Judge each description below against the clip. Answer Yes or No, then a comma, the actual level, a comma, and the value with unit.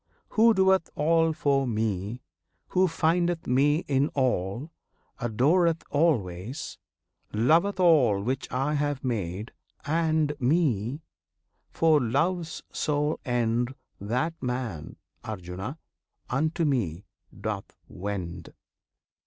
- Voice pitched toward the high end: No, low, 135 Hz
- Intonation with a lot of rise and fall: Yes, wide, 6.4 semitones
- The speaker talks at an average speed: No, slow, 95 wpm